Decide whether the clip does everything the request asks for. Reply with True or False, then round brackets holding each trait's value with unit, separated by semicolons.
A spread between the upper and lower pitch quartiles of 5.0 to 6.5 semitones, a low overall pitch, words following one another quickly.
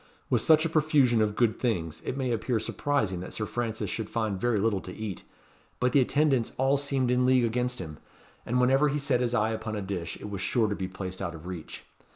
False (4.3 semitones; 115 Hz; 230 wpm)